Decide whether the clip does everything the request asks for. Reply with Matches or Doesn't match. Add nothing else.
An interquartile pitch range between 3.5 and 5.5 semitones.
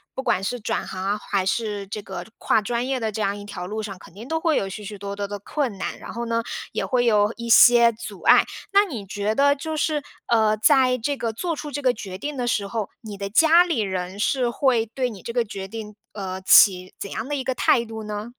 Matches